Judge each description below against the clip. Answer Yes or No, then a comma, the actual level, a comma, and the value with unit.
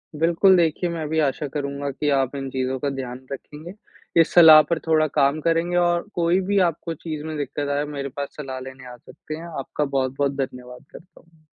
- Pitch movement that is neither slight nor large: Yes, average, 3.3 semitones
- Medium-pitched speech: Yes, medium, 150 Hz